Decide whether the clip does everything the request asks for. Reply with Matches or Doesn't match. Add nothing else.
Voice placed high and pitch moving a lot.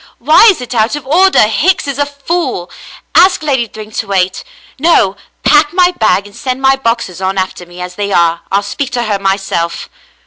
Matches